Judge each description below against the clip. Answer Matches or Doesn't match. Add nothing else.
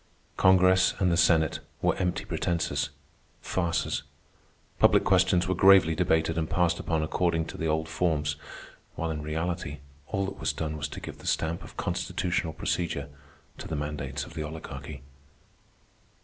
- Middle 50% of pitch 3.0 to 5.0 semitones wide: Doesn't match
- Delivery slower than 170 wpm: Matches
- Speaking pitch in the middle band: Doesn't match